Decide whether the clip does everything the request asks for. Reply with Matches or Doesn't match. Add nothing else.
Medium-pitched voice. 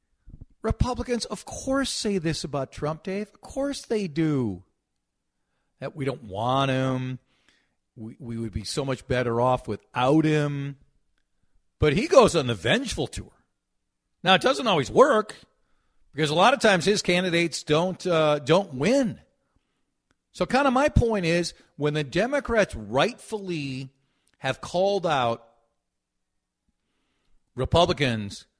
Matches